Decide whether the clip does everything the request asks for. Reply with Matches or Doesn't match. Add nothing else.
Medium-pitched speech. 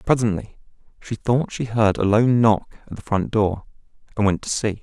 Doesn't match